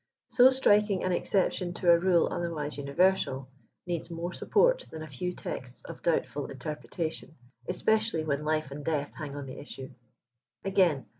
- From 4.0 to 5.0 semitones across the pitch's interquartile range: Yes, average, 4.3 semitones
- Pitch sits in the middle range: Yes, medium, 165 Hz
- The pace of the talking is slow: No, average, 160 wpm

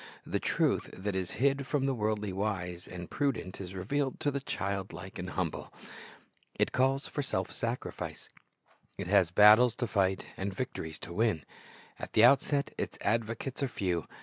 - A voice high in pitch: No, low, 105 Hz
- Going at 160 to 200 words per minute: Yes, average, 170 wpm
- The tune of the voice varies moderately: No, wide, 5.7 semitones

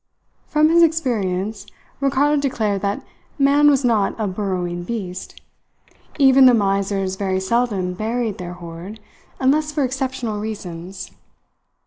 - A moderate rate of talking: No, slow, 120 wpm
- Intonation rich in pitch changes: Yes, wide, 5.9 semitones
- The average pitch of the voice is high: Yes, high, 215 Hz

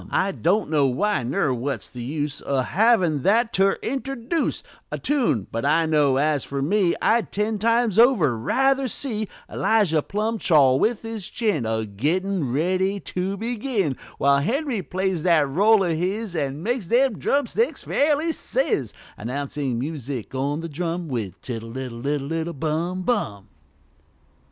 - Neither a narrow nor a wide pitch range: No, wide, 7.8 semitones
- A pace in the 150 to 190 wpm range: Yes, average, 155 wpm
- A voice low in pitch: No, medium, 175 Hz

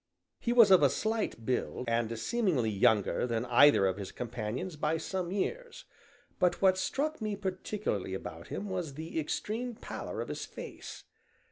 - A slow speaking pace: No, average, 160 wpm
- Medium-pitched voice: Yes, medium, 165 Hz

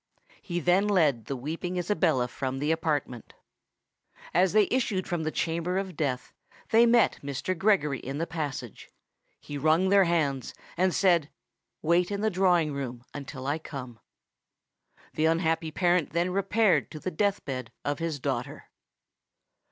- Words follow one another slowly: No, average, 150 wpm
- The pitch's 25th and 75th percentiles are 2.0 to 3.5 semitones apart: No, average, 4.5 semitones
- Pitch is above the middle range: No, medium, 165 Hz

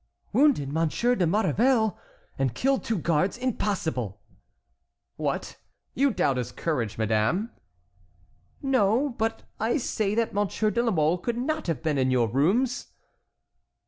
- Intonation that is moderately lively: No, wide, 8.4 semitones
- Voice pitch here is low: No, high, 200 Hz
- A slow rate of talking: Yes, slow, 130 wpm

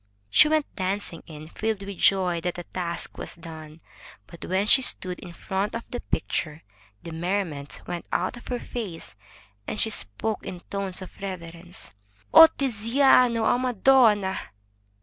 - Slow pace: No, average, 160 wpm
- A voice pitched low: No, high, 190 Hz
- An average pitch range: Yes, average, 4.6 semitones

